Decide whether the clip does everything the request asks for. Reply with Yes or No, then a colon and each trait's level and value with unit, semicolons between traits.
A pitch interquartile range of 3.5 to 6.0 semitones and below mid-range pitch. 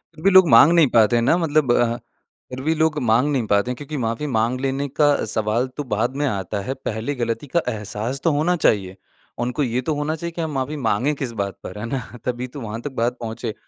Yes: average, 4.5 semitones; low, 125 Hz